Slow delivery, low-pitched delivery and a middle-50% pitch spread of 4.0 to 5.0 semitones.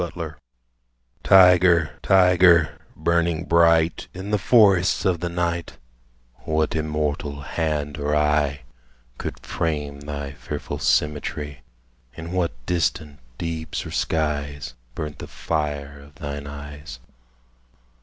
No: slow, 115 wpm; very low, 80 Hz; average, 2.9 semitones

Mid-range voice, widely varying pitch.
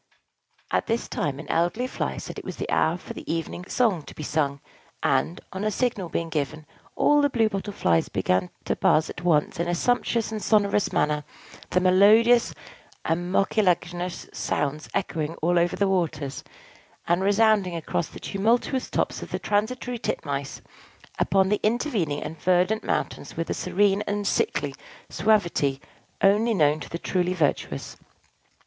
No: medium, 180 Hz; average, 5.0 semitones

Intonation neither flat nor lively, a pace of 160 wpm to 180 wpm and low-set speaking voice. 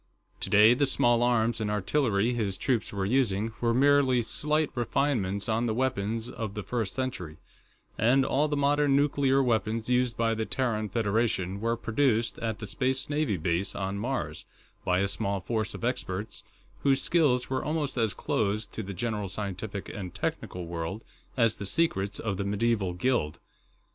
Yes: average, 4.4 semitones; average, 170 wpm; low, 115 Hz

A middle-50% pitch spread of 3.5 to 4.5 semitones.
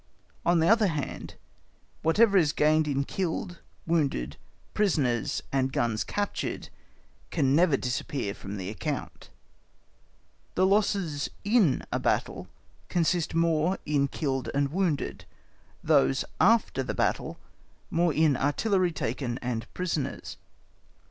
No: average, 5.0 semitones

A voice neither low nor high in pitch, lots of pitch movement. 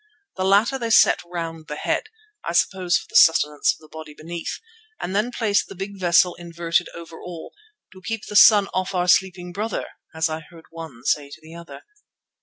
No: medium, 175 Hz; average, 3.1 semitones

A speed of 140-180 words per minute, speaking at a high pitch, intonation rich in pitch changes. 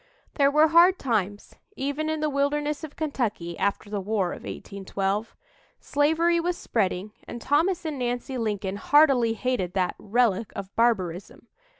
Yes: average, 145 wpm; high, 240 Hz; wide, 6.8 semitones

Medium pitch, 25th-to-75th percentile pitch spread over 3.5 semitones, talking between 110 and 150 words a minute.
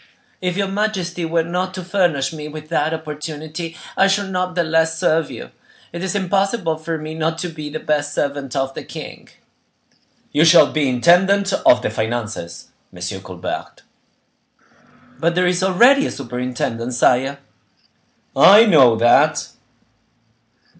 Yes: medium, 160 Hz; average, 4.3 semitones; average, 145 wpm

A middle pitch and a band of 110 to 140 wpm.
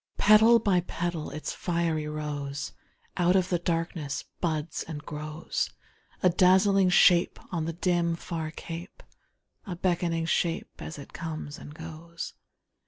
Yes: medium, 170 Hz; slow, 135 wpm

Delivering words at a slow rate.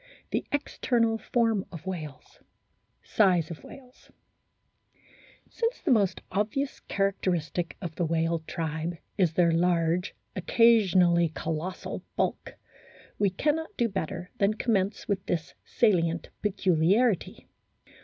Yes: slow, 110 wpm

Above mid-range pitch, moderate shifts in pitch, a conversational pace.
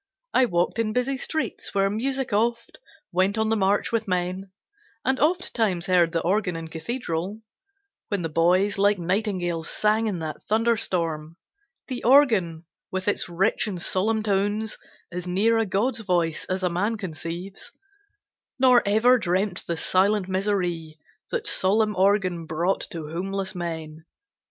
Yes: high, 195 Hz; average, 4.0 semitones; average, 145 wpm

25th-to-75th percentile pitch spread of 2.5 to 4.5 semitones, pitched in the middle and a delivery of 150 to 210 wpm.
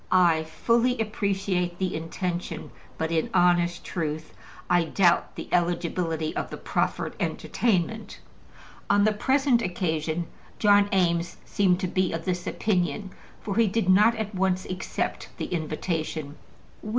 No: average, 3.2 semitones; medium, 180 Hz; slow, 135 wpm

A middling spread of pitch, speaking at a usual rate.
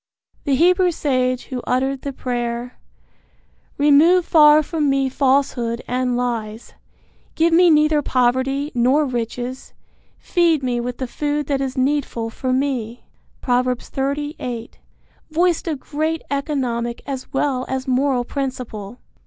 No: average, 3.0 semitones; slow, 130 wpm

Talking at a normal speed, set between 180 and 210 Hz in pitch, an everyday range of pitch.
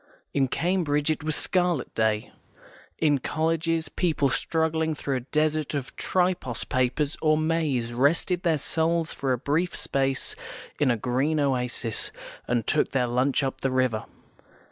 No: average, 150 wpm; medium, 145 Hz; average, 3.8 semitones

